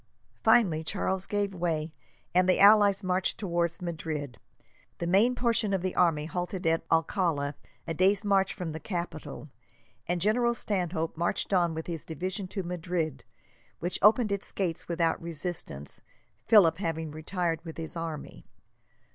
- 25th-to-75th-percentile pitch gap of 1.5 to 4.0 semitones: Yes, average, 3.1 semitones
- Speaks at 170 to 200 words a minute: No, average, 145 wpm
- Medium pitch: Yes, medium, 175 Hz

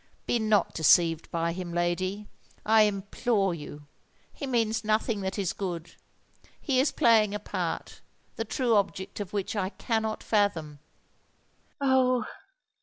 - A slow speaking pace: Yes, slow, 125 wpm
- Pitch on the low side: No, high, 205 Hz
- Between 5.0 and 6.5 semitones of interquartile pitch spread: No, average, 3.9 semitones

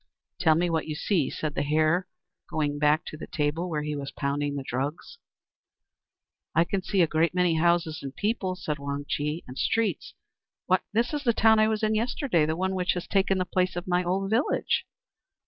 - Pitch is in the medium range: Yes, medium, 170 Hz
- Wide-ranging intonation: No, average, 4.1 semitones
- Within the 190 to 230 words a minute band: Yes, fast, 205 wpm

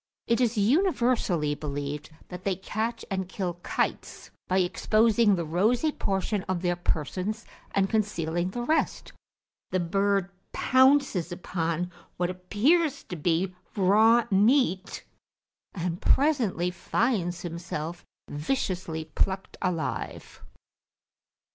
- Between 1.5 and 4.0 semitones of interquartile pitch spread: No, average, 4.5 semitones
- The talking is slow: Yes, slow, 110 wpm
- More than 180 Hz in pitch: Yes, high, 190 Hz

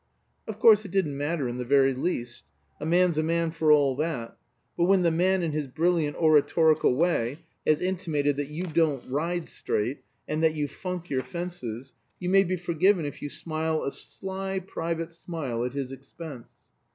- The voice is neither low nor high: Yes, medium, 160 Hz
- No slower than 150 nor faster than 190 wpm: Yes, average, 185 wpm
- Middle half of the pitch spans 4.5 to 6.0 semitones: No, average, 3.8 semitones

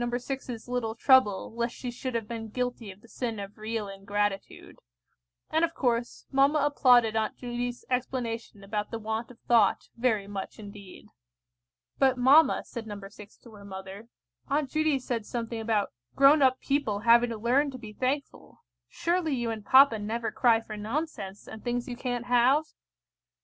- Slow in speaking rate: No, average, 170 wpm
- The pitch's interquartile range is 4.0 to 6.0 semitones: No, average, 3.2 semitones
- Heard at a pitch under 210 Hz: No, high, 235 Hz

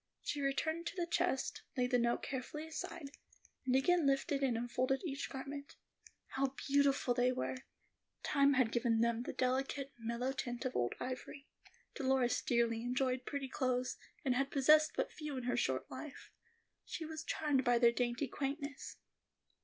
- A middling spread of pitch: No, narrow, 2.3 semitones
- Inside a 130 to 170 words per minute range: Yes, average, 165 wpm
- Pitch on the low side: No, very high, 265 Hz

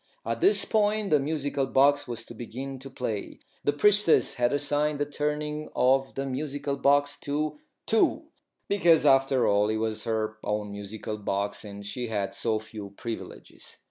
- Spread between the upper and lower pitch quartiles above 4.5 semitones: Yes, average, 5.1 semitones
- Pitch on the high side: No, low, 135 Hz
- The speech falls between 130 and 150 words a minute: No, average, 165 wpm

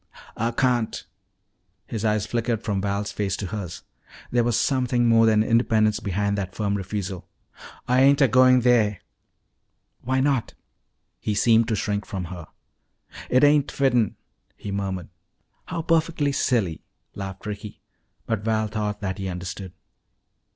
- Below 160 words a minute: Yes, average, 145 wpm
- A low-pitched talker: Yes, low, 110 Hz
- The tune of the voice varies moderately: Yes, average, 3.5 semitones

